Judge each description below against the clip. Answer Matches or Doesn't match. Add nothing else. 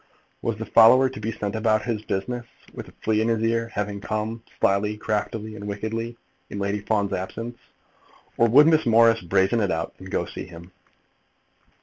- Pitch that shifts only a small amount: Matches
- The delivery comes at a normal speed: Matches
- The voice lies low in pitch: Matches